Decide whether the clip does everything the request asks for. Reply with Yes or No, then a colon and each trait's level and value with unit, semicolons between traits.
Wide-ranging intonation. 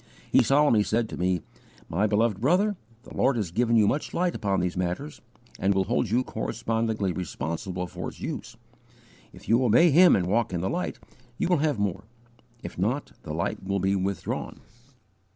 No: average, 4.7 semitones